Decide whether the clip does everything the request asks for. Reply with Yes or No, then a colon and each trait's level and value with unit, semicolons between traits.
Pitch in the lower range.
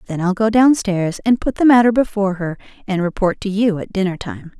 No: high, 205 Hz